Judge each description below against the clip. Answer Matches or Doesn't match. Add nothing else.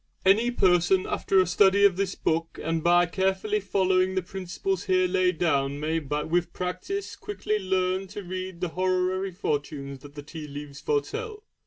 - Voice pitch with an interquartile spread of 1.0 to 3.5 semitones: Matches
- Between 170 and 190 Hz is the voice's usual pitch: Matches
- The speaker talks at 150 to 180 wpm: Matches